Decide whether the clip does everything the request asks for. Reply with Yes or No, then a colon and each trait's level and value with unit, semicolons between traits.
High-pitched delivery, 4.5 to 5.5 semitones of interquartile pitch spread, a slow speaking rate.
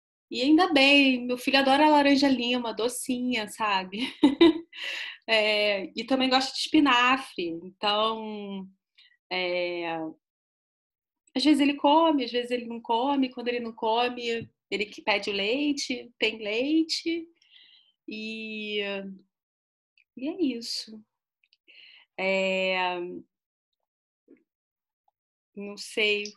Yes: high, 240 Hz; average, 5.2 semitones; slow, 100 wpm